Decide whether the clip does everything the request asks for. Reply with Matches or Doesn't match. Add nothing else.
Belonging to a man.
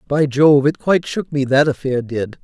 Matches